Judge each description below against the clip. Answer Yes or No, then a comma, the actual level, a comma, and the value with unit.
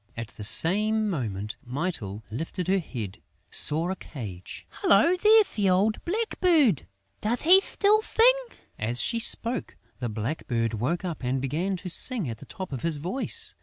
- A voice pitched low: No, medium, 175 Hz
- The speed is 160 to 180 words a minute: Yes, average, 165 wpm